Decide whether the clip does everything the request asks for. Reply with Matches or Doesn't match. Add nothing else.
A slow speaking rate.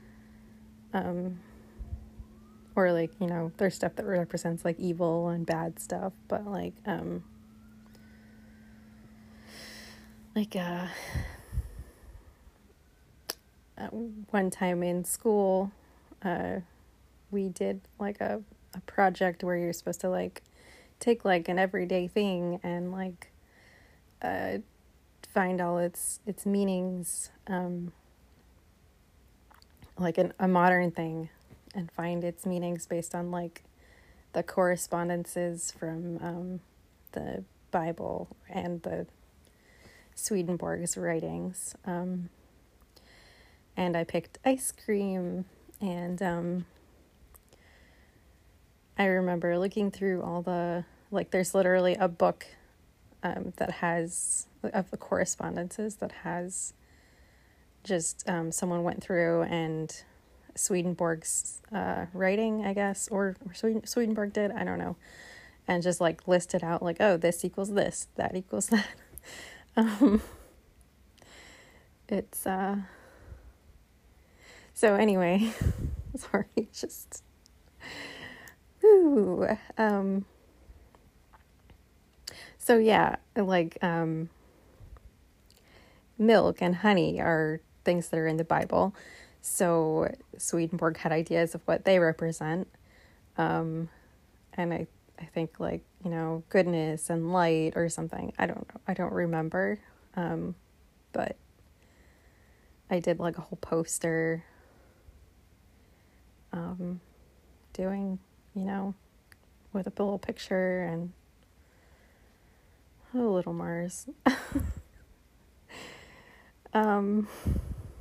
Matches